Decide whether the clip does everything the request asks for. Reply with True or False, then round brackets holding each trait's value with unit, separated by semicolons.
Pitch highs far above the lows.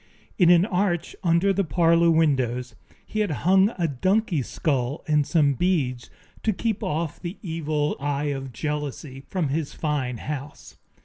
False (4.0 semitones)